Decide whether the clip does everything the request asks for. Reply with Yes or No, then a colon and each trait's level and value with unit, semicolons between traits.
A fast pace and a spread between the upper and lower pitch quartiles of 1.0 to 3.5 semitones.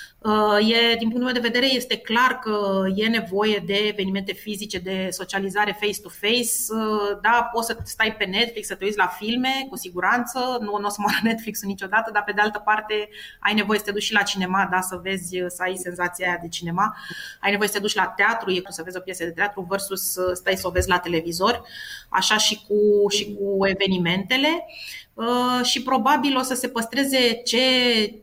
Yes: fast, 200 wpm; average, 3.1 semitones